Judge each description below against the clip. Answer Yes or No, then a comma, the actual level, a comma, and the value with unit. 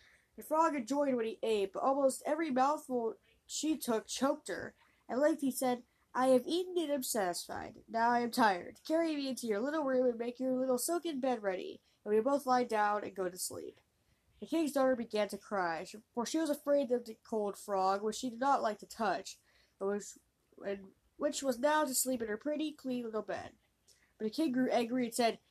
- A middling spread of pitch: Yes, average, 4.9 semitones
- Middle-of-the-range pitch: No, very high, 255 Hz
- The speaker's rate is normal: No, fast, 215 wpm